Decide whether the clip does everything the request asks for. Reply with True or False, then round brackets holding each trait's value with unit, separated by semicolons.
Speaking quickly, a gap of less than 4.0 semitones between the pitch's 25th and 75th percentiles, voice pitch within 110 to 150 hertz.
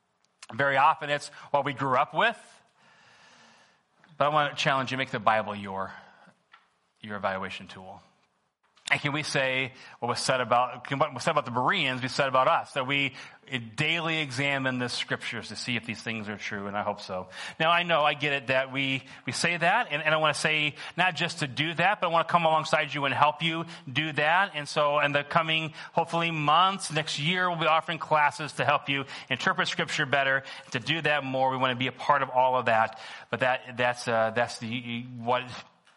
True (220 wpm; 3.6 semitones; 140 Hz)